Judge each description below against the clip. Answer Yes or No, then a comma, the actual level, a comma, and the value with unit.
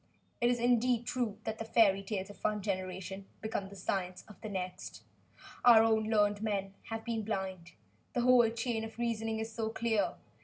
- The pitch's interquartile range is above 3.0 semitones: No, narrow, 2.6 semitones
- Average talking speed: Yes, average, 185 wpm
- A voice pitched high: Yes, high, 220 Hz